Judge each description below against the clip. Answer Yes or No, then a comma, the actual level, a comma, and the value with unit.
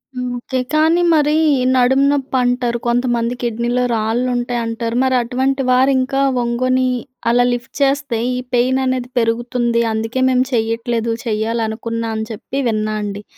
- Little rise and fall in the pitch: Yes, narrow, 2.0 semitones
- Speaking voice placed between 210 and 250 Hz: Yes, high, 240 Hz